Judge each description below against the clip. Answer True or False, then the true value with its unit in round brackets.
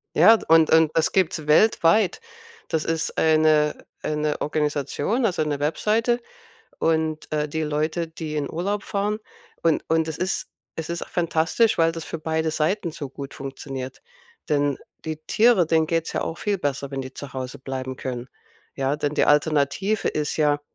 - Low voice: False (155 Hz)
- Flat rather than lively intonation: True (2.3 semitones)